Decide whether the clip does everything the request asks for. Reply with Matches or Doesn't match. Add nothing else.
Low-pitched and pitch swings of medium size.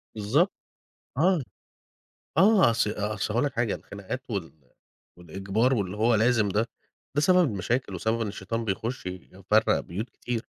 Matches